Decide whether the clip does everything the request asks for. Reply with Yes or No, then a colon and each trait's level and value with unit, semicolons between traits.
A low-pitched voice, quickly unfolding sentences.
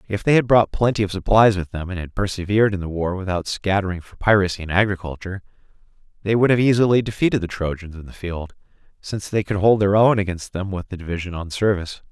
Yes: very low, 95 Hz; fast, 220 wpm